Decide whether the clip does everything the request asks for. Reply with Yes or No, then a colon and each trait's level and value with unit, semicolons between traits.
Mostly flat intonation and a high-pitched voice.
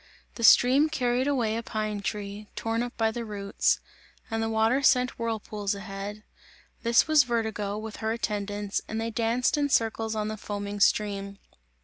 Yes: narrow, 2.2 semitones; high, 220 Hz